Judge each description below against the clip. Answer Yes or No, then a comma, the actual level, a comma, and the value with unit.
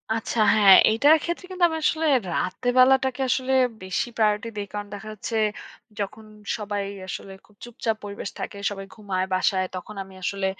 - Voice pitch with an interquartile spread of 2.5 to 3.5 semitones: No, average, 3.9 semitones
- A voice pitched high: Yes, high, 210 Hz